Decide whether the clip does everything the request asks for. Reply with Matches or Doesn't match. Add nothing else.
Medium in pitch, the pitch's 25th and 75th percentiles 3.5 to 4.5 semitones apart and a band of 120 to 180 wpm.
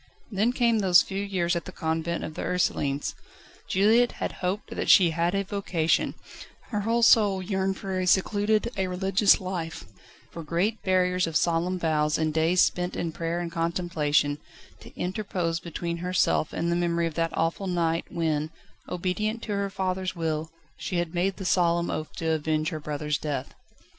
Doesn't match